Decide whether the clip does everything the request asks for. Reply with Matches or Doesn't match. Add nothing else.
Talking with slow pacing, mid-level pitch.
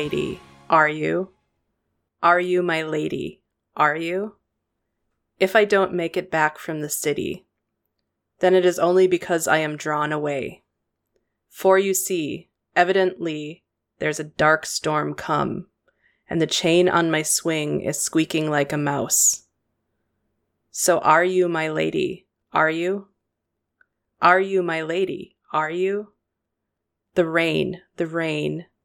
Matches